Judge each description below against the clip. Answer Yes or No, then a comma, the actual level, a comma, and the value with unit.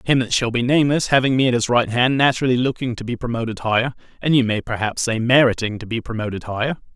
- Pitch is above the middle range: No, low, 120 Hz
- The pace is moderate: No, fast, 235 wpm